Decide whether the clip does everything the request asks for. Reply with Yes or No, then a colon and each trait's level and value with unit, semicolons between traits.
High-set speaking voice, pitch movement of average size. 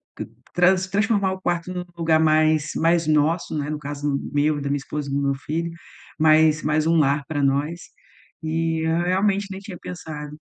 No: medium, 160 Hz; average, 3.0 semitones